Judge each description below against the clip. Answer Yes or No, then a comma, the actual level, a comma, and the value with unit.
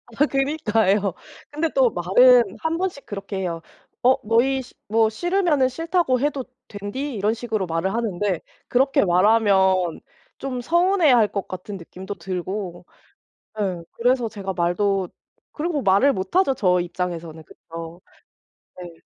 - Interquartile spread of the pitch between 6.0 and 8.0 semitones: Yes, wide, 6.3 semitones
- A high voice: Yes, high, 210 Hz